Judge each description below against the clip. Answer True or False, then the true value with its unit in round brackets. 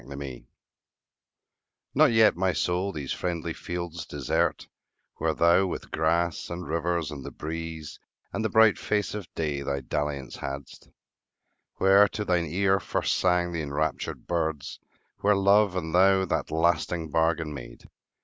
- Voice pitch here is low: True (85 Hz)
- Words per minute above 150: False (145 wpm)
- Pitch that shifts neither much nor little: True (3.6 semitones)